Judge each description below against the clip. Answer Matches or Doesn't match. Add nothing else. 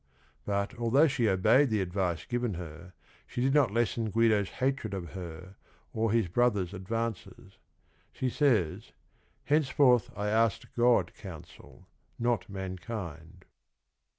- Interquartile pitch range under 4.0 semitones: Doesn't match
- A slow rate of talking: Matches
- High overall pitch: Doesn't match